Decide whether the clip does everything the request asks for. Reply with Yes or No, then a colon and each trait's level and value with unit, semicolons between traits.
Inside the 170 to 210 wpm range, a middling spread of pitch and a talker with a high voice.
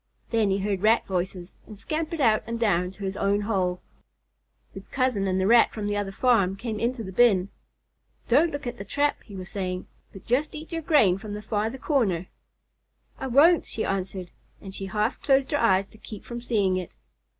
Yes: fast, 205 wpm; average, 4.2 semitones; high, 210 Hz